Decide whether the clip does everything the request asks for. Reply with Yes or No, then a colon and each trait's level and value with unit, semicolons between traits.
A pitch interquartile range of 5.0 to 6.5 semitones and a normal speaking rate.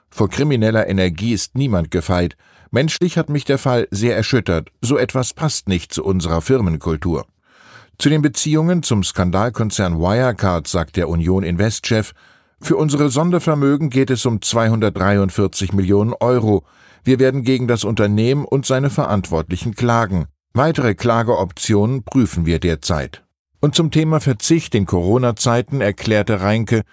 Yes: wide, 5.6 semitones; average, 135 wpm